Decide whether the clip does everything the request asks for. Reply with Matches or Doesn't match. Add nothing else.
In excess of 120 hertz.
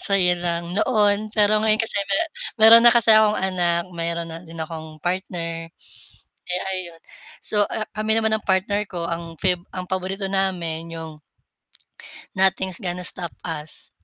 Matches